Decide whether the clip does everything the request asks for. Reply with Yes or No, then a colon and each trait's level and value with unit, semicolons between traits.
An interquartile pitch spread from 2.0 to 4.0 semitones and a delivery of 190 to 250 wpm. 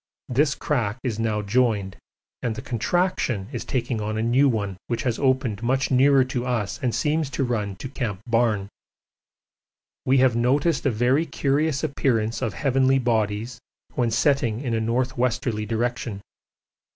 No: average, 3.2 semitones; average, 160 wpm